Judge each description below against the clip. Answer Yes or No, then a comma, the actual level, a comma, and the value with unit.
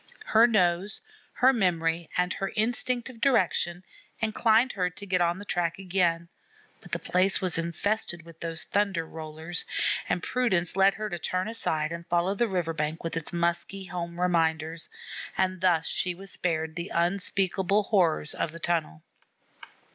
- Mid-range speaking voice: Yes, medium, 180 Hz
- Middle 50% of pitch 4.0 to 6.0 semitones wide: No, average, 2.8 semitones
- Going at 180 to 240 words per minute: No, average, 160 wpm